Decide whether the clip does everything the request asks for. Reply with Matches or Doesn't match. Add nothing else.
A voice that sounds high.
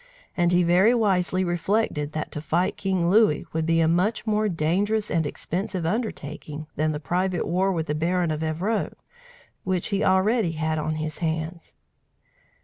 Doesn't match